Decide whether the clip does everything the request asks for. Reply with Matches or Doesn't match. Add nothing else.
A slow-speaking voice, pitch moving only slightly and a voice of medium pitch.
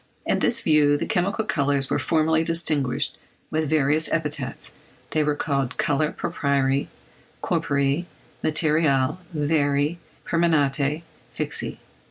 Matches